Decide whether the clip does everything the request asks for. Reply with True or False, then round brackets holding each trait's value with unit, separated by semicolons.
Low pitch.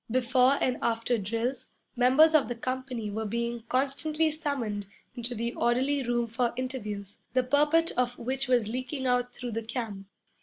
False (245 Hz)